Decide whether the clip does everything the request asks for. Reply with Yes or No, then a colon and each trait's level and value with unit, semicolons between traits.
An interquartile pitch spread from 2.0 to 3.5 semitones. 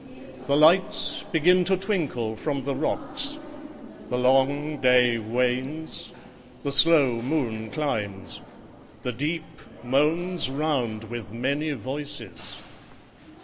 No: average, 4.4 semitones